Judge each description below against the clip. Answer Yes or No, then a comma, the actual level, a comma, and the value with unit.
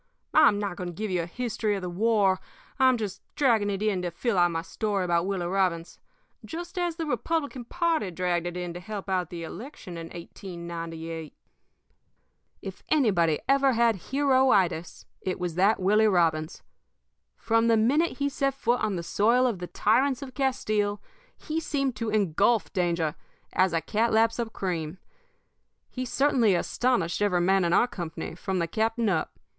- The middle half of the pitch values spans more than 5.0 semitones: Yes, wide, 5.6 semitones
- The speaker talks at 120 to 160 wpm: No, average, 175 wpm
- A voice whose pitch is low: No, high, 205 Hz